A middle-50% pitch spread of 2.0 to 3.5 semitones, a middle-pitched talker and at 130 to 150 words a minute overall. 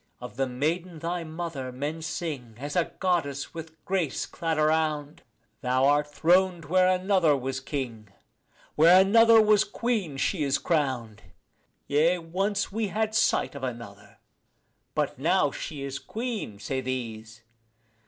No: wide, 5.6 semitones; medium, 155 Hz; average, 140 wpm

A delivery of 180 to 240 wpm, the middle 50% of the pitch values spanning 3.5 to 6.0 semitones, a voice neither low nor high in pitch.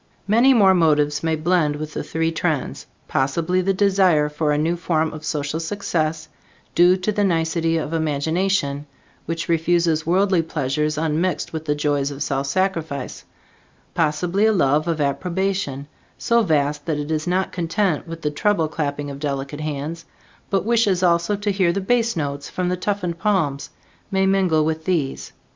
No: average, 165 wpm; average, 3.8 semitones; medium, 165 Hz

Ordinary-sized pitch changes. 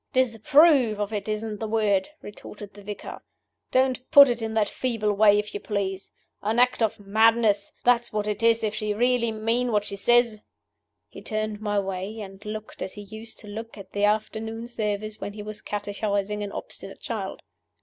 No: narrow, 1.7 semitones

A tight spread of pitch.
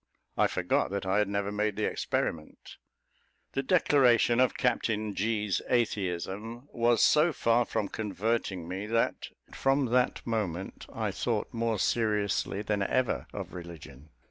No: average, 3.4 semitones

